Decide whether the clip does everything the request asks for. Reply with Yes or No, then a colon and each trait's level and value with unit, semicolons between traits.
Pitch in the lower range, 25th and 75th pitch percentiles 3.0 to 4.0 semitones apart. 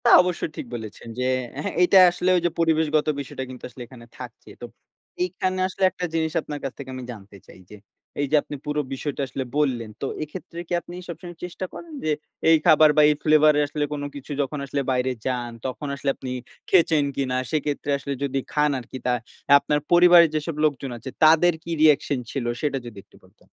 No: medium, 150 Hz; average, 3.6 semitones